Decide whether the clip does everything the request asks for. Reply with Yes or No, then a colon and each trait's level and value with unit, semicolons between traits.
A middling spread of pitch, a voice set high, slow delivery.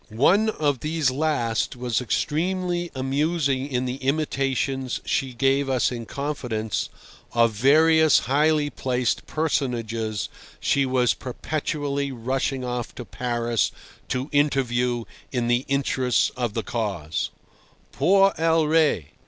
No: average, 3.7 semitones; low, 130 Hz; slow, 115 wpm